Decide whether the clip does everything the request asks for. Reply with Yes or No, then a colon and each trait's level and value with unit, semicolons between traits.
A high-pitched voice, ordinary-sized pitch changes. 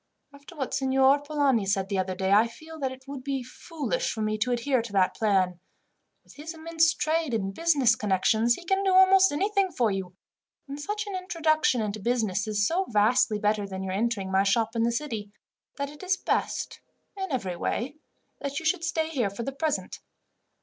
No: very high, 260 Hz; wide, 7.2 semitones